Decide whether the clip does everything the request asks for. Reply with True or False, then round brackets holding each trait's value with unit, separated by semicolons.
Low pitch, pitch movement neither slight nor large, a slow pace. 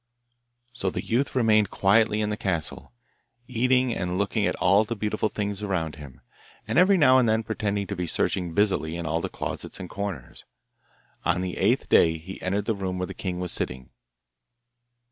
False (100 Hz; 3.6 semitones; 185 wpm)